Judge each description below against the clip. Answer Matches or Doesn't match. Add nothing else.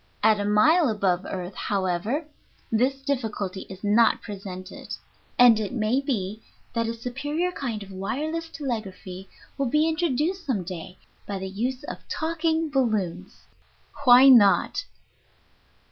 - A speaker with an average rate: Doesn't match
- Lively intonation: Matches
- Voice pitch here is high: Matches